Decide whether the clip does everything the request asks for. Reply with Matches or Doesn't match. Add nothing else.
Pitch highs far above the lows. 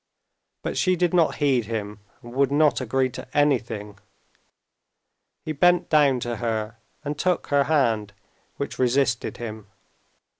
Doesn't match